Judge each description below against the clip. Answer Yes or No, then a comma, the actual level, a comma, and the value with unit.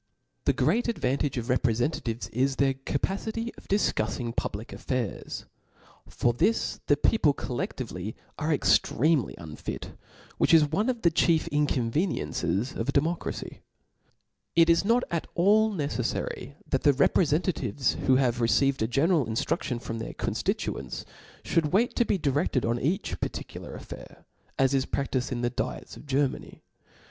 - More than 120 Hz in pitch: Yes, medium, 140 Hz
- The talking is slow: No, average, 150 wpm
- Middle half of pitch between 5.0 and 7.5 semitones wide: Yes, wide, 5.5 semitones